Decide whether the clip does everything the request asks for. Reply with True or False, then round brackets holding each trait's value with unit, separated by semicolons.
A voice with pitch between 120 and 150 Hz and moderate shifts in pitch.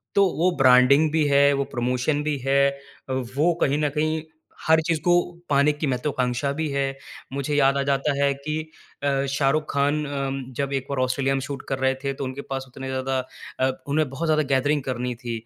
False (140 Hz; 1.9 semitones)